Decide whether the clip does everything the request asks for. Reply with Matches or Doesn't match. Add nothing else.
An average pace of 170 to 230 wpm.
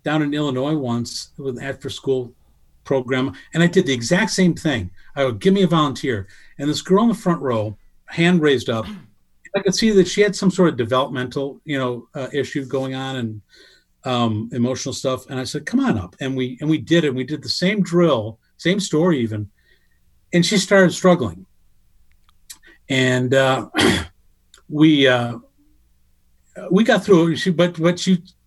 Matches